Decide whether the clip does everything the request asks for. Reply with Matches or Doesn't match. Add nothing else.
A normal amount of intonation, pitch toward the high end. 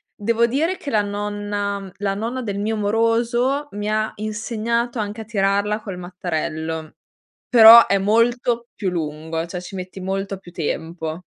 Matches